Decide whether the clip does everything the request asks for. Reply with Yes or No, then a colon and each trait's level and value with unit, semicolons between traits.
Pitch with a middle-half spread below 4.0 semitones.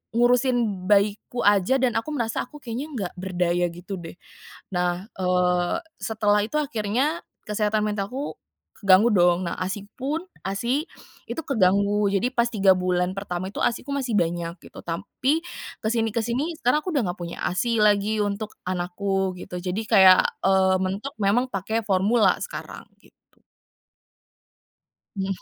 No: average, 4.3 semitones